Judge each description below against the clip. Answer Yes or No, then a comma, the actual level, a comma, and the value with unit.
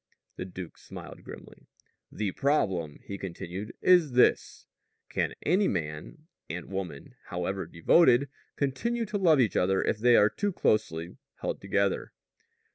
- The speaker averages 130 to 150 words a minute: Yes, slow, 135 wpm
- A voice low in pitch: Yes, low, 100 Hz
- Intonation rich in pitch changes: Yes, wide, 8.0 semitones